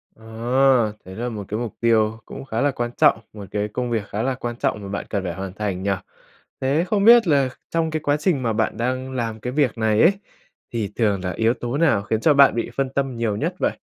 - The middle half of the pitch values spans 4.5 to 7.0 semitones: No, average, 4.1 semitones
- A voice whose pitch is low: Yes, low, 115 Hz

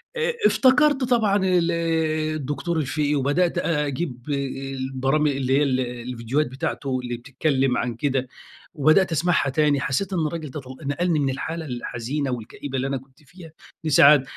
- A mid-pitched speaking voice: Yes, medium, 145 Hz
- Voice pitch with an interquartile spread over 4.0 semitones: No, average, 3.7 semitones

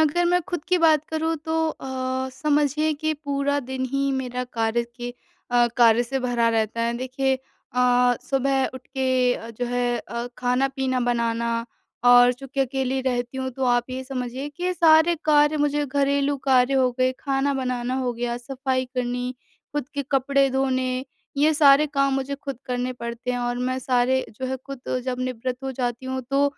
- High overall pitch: Yes, very high, 260 Hz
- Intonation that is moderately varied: No, narrow, 2.1 semitones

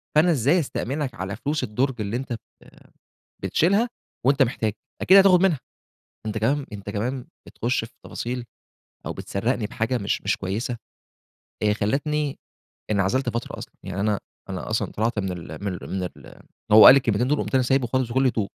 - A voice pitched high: No, low, 120 Hz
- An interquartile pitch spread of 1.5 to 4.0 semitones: No, average, 4.7 semitones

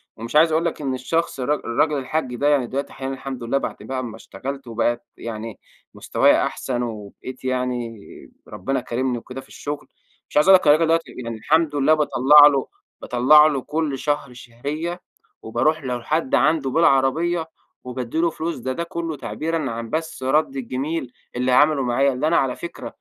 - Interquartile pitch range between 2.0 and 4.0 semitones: Yes, average, 3.7 semitones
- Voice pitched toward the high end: No, low, 135 Hz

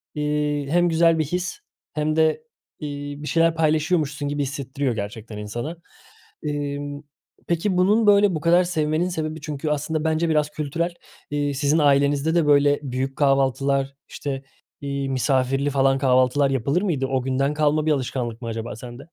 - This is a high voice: No, medium, 145 Hz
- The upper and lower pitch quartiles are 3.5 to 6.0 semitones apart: No, average, 2.7 semitones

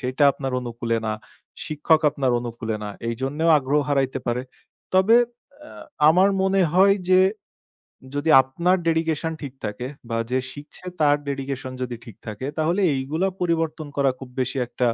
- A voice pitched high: No, medium, 140 Hz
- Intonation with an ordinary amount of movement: Yes, average, 4.2 semitones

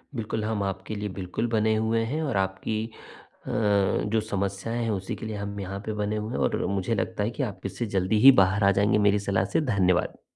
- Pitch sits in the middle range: No, low, 105 Hz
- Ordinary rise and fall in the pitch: No, narrow, 2.2 semitones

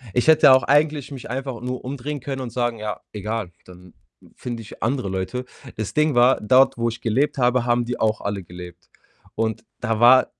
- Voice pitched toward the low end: Yes, low, 120 Hz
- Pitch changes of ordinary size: Yes, average, 3.2 semitones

